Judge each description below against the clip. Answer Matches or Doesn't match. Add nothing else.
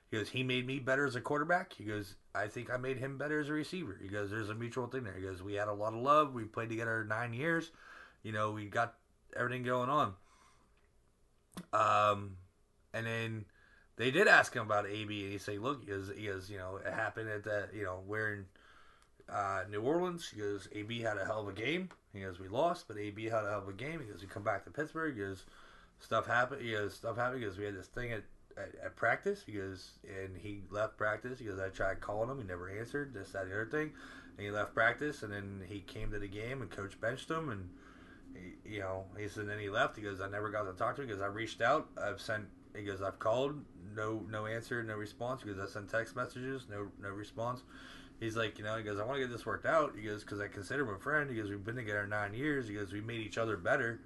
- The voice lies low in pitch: Matches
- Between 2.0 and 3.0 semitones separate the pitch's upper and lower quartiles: Doesn't match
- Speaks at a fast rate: Matches